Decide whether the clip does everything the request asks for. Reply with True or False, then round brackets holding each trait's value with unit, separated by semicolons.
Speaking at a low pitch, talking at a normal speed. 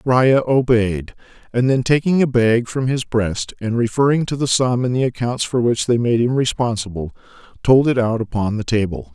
True (120 Hz; 195 wpm)